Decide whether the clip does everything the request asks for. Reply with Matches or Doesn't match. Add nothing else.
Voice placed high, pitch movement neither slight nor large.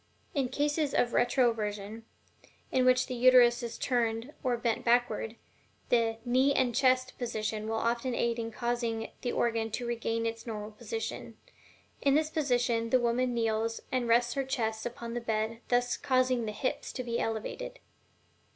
Doesn't match